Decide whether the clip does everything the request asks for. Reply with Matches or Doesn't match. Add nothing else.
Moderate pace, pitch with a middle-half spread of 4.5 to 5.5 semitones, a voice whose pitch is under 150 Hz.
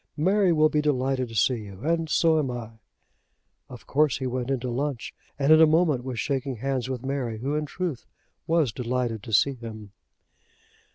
Doesn't match